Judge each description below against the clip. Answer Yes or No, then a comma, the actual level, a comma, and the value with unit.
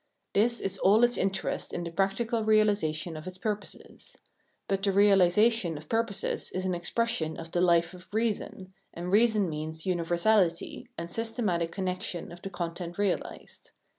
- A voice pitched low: No, medium, 185 Hz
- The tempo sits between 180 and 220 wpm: No, average, 160 wpm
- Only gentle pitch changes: No, average, 3.8 semitones